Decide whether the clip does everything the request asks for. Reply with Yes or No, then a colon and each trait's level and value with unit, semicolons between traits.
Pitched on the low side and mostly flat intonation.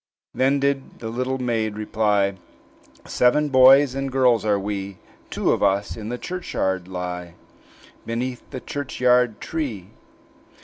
No: low, 120 Hz; average, 4.5 semitones